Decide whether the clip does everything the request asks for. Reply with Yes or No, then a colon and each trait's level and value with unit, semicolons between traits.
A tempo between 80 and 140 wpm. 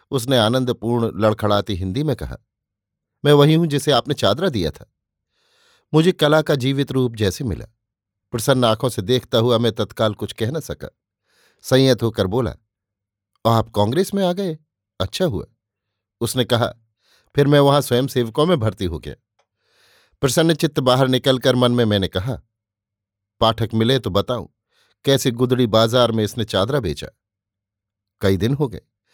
No: average, 155 wpm